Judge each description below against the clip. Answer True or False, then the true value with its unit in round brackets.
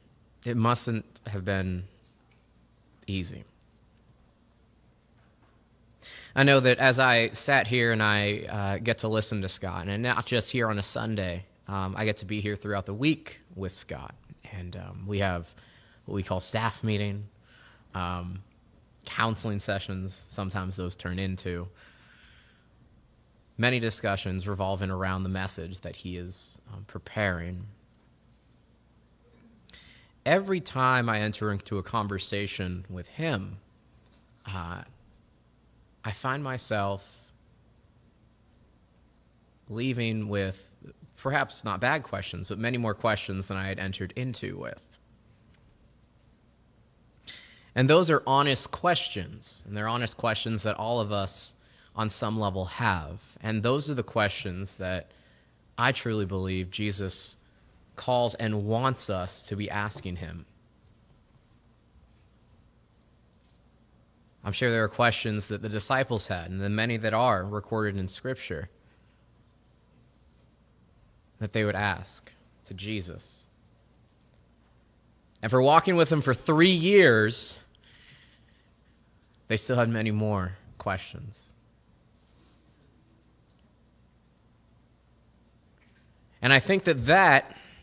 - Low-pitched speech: True (105 Hz)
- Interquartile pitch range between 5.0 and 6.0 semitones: False (3.4 semitones)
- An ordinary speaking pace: False (115 wpm)